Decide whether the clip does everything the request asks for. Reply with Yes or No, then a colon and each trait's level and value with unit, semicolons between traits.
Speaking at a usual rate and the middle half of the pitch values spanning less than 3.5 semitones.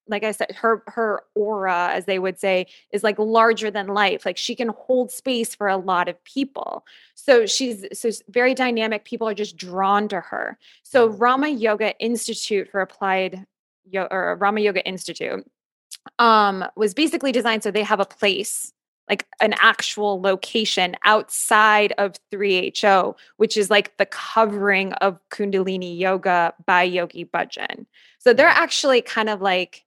Yes: average, 160 wpm; average, 3.0 semitones